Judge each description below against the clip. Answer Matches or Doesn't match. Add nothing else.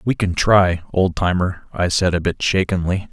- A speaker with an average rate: Matches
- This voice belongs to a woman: Doesn't match